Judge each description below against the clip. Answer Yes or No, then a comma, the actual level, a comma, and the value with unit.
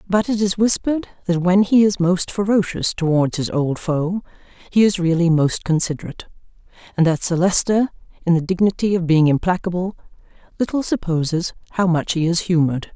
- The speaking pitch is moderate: Yes, medium, 180 Hz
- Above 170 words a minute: No, average, 165 wpm